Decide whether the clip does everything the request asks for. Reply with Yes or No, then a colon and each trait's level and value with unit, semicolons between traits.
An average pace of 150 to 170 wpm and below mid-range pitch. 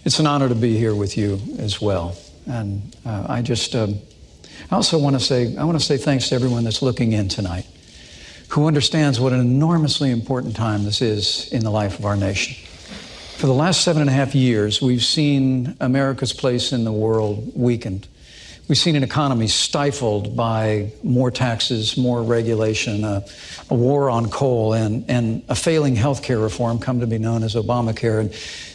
No: average, 185 wpm; low, 120 Hz